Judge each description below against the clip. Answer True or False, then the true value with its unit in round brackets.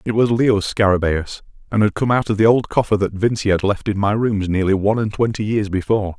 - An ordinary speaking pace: False (245 wpm)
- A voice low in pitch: True (105 Hz)